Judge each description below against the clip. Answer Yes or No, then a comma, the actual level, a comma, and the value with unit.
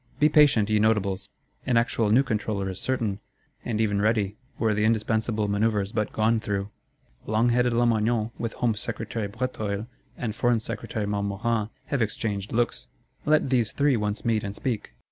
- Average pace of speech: Yes, average, 165 wpm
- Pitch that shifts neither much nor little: No, narrow, 2.3 semitones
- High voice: No, low, 110 Hz